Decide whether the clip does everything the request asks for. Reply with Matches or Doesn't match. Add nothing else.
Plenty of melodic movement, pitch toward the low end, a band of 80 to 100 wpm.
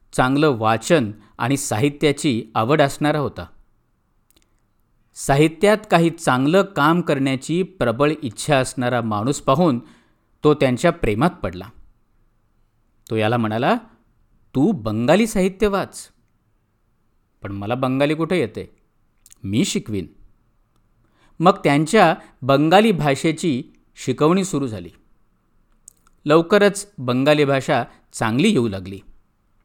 Matches